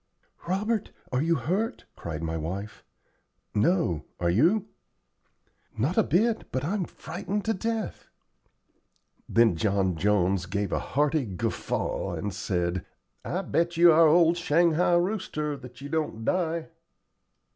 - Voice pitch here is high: No, medium, 150 Hz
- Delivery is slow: Yes, slow, 130 wpm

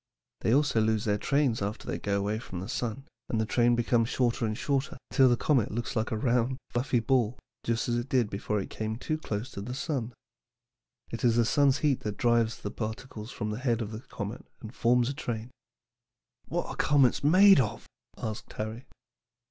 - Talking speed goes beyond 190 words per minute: Yes, average, 200 wpm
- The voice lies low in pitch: Yes, low, 115 Hz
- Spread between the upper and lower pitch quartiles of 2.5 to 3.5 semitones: Yes, average, 3.0 semitones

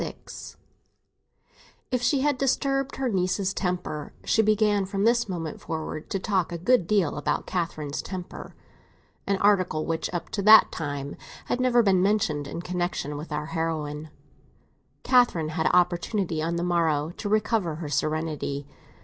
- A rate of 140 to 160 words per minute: Yes, average, 145 wpm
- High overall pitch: No, medium, 180 Hz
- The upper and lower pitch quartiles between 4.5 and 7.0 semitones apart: Yes, average, 5.1 semitones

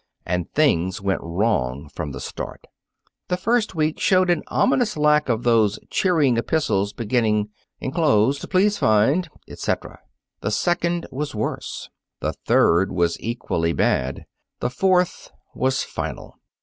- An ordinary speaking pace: No, slow, 130 wpm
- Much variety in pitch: Yes, wide, 8.8 semitones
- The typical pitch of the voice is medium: No, low, 125 Hz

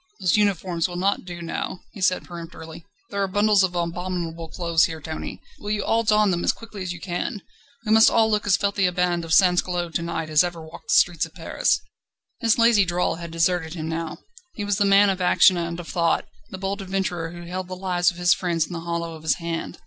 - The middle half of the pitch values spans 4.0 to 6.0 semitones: No, narrow, 2.6 semitones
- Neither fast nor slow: No, fast, 235 wpm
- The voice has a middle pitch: Yes, medium, 180 Hz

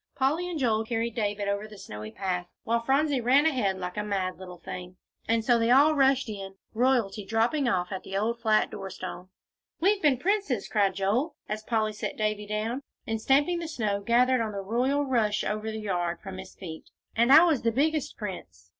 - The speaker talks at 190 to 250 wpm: Yes, fast, 205 wpm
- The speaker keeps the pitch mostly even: No, average, 5.0 semitones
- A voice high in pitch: Yes, high, 220 Hz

